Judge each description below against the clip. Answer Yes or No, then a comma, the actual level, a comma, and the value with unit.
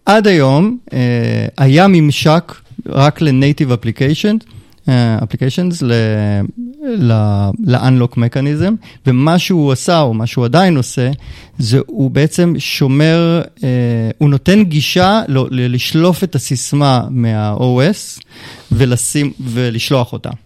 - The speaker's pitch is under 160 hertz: Yes, low, 135 Hz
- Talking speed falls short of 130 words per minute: Yes, slow, 100 wpm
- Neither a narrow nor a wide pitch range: Yes, average, 5.0 semitones